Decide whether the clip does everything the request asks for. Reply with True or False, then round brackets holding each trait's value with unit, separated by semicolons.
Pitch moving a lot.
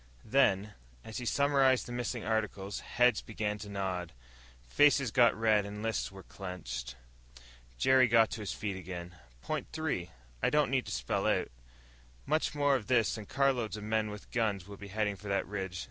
False (4.0 semitones)